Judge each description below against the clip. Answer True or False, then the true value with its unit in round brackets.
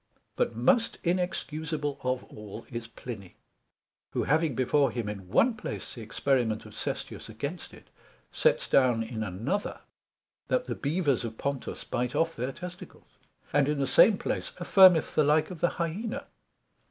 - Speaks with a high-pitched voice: False (140 Hz)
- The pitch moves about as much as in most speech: False (6.9 semitones)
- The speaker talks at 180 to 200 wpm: False (155 wpm)